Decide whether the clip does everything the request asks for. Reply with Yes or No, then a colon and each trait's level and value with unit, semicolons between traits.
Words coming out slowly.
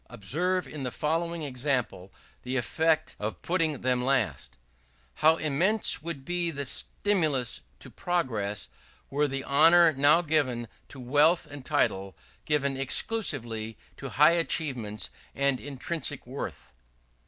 Yes: slow, 125 wpm